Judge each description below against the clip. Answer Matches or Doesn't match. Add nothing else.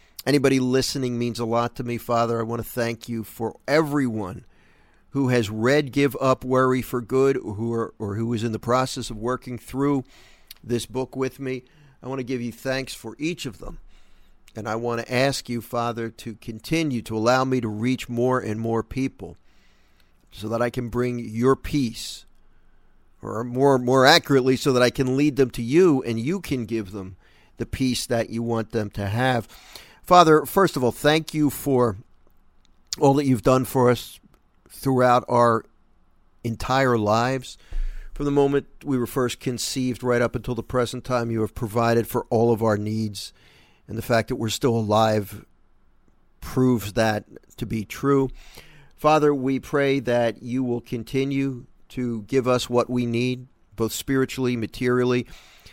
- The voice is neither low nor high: Doesn't match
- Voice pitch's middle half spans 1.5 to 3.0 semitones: Matches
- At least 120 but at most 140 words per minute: Doesn't match